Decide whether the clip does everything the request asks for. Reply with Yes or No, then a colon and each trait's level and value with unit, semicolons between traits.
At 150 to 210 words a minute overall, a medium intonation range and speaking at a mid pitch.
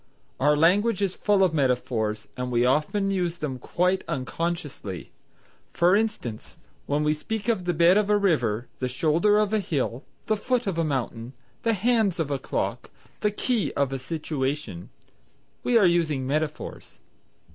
No: average, 170 wpm; wide, 7.1 semitones; medium, 165 Hz